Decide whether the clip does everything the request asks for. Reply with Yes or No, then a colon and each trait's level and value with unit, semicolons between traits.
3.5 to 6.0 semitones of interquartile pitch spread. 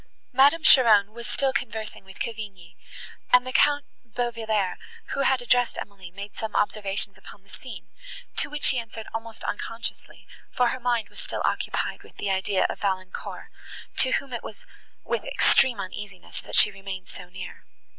Yes: average, 4.0 semitones